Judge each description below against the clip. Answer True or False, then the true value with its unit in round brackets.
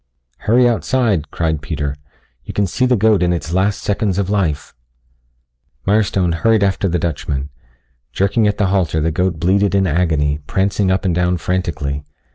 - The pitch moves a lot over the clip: False (3.7 semitones)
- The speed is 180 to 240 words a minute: False (165 wpm)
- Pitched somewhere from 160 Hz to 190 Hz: False (95 Hz)